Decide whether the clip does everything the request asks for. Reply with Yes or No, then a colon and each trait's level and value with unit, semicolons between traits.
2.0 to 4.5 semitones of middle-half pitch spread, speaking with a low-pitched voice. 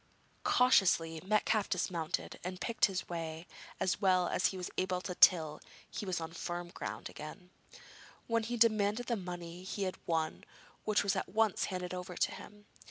No: average, 2.9 semitones; medium, 185 Hz